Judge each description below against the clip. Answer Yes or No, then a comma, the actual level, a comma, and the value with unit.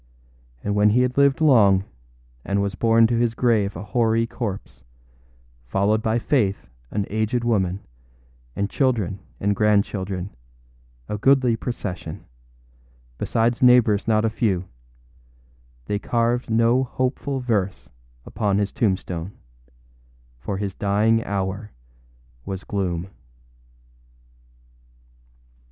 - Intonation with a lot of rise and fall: No, average, 3.1 semitones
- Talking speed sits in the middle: No, slow, 110 wpm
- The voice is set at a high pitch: No, low, 105 Hz